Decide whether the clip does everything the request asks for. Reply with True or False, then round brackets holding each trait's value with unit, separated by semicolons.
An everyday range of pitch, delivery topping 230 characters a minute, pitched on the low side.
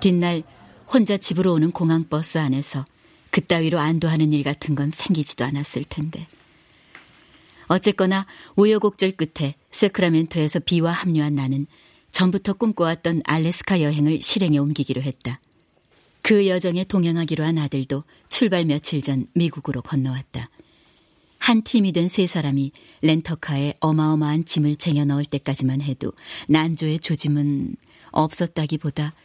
False (3.3 semitones; 310 characters per minute; 155 Hz)